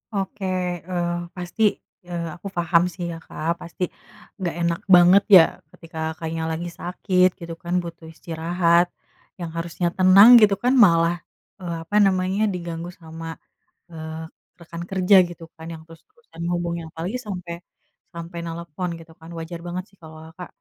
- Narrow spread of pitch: Yes, narrow, 1.8 semitones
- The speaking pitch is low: No, medium, 170 Hz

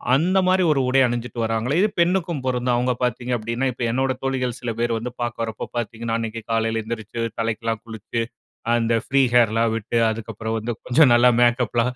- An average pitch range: No, narrow, 2.0 semitones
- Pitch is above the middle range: No, low, 120 Hz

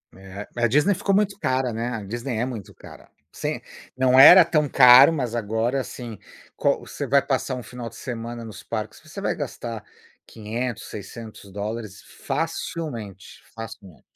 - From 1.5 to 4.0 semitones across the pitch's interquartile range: Yes, average, 3.3 semitones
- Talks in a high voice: No, low, 120 Hz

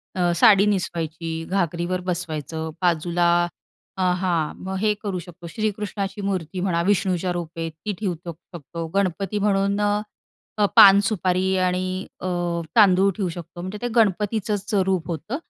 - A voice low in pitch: No, medium, 185 Hz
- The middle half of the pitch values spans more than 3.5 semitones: No, average, 2.7 semitones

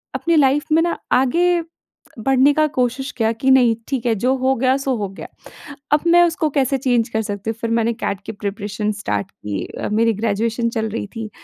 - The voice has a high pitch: Yes, high, 240 Hz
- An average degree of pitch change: Yes, average, 3.6 semitones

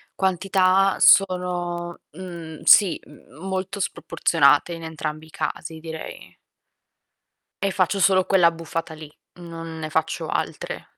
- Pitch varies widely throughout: No, average, 2.7 semitones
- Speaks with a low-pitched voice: No, medium, 170 Hz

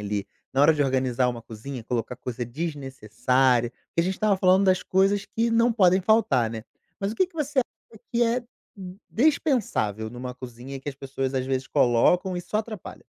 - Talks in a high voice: No, medium, 140 Hz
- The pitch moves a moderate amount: No, wide, 8.3 semitones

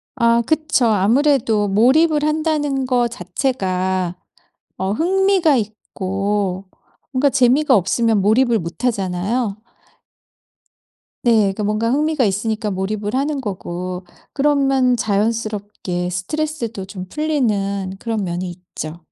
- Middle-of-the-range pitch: No, high, 220 Hz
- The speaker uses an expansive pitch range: Yes, wide, 5.9 semitones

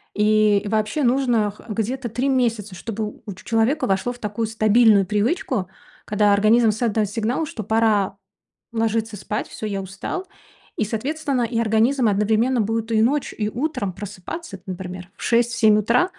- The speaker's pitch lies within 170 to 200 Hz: No, high, 220 Hz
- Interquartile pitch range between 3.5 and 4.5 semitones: No, narrow, 2.5 semitones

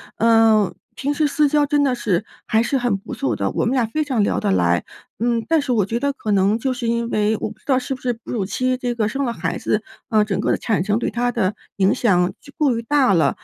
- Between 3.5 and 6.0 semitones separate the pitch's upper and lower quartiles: Yes, average, 3.8 semitones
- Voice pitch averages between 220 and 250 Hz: Yes, high, 230 Hz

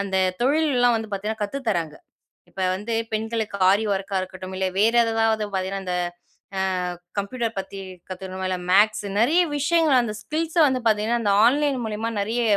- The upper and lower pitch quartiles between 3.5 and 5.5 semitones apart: Yes, average, 3.9 semitones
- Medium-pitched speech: No, high, 220 Hz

